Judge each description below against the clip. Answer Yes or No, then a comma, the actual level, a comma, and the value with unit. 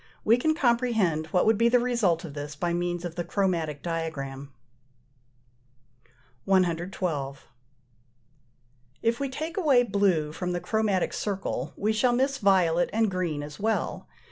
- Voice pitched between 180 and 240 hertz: Yes, medium, 185 Hz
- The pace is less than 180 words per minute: Yes, average, 140 wpm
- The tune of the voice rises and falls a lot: Yes, wide, 5.9 semitones